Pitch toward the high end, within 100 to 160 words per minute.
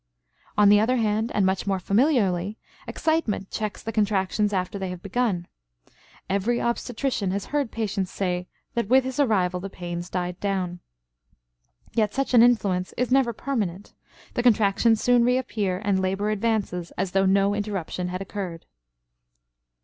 Yes: high, 205 Hz; average, 150 wpm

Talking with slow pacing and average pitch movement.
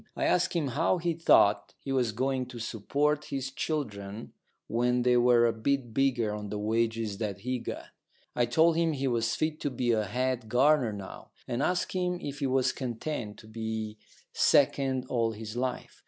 No: average, 185 wpm; average, 3.8 semitones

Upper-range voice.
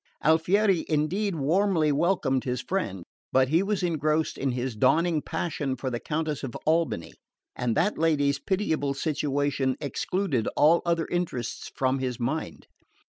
No: medium, 150 Hz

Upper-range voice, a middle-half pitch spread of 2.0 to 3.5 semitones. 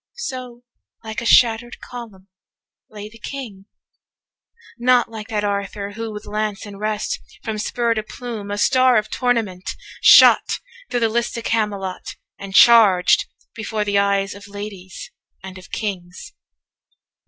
Yes: high, 215 Hz; narrow, 2.5 semitones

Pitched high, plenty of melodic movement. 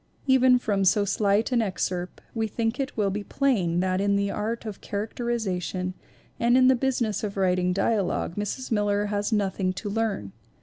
No: high, 205 Hz; average, 3.2 semitones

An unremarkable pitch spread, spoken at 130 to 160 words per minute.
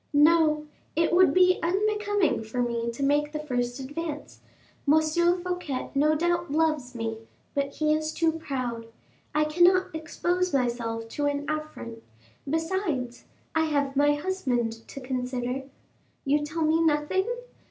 Yes: average, 4.6 semitones; average, 140 wpm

